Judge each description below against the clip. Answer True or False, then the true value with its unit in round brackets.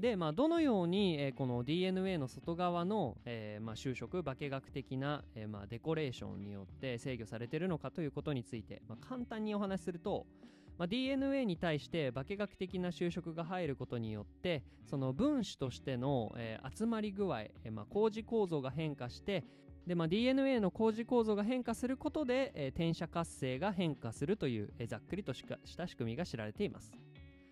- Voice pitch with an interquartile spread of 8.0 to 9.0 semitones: True (8.3 semitones)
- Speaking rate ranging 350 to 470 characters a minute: True (385 characters per minute)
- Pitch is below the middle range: False (160 Hz)